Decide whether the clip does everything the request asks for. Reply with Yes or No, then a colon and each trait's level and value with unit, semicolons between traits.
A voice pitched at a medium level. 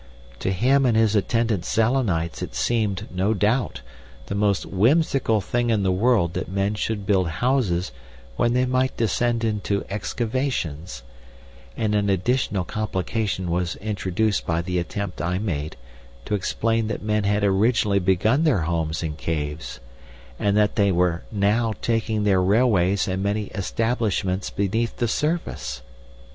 No: low, 105 Hz